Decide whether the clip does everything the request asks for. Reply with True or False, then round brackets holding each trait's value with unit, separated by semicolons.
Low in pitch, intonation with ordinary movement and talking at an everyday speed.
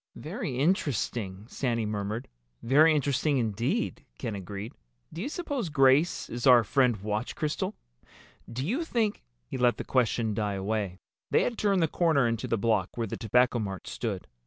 False (120 Hz; 5.8 semitones; 165 wpm)